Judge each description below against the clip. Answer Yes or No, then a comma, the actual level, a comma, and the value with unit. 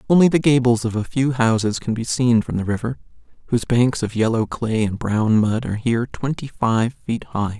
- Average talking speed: No, fast, 215 wpm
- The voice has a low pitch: Yes, low, 115 Hz